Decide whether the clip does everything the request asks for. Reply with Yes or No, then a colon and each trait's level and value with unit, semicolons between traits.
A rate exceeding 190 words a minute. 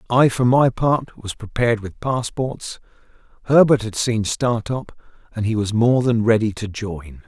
No: average, 165 wpm